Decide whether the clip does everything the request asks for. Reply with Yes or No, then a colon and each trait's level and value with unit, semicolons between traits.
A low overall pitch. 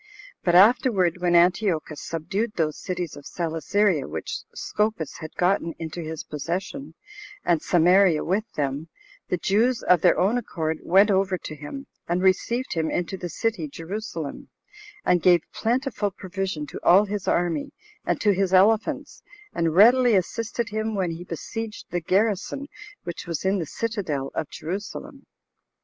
No: medium, 185 Hz